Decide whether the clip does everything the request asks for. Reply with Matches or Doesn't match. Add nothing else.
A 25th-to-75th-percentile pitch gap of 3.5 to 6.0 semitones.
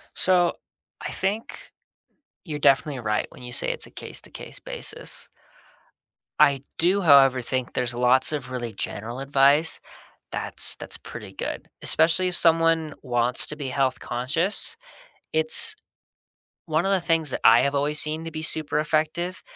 Matches